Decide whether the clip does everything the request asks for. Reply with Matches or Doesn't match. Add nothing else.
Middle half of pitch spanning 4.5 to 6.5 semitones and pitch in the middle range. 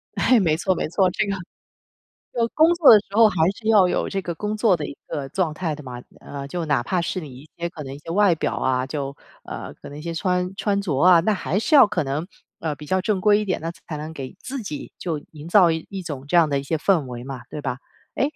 Matches